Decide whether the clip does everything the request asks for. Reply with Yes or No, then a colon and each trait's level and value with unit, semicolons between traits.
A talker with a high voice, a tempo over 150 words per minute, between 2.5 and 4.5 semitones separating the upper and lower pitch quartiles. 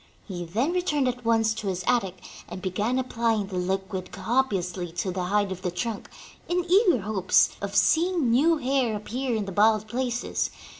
No: high, 220 Hz; average, 180 wpm; average, 5.0 semitones